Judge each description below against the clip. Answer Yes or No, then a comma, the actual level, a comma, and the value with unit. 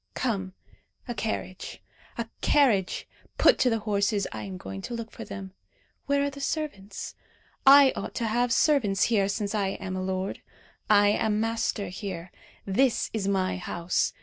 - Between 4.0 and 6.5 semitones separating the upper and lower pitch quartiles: No, average, 3.5 semitones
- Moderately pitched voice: No, high, 205 Hz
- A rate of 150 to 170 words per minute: Yes, average, 165 wpm